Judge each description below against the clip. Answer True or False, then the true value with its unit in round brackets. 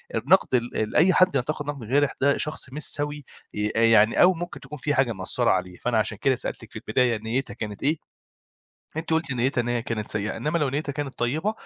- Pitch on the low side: True (130 Hz)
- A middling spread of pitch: True (4.6 semitones)